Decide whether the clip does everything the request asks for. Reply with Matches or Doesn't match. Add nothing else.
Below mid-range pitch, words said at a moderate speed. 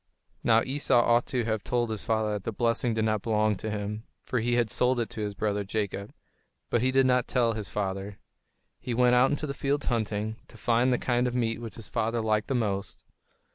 Doesn't match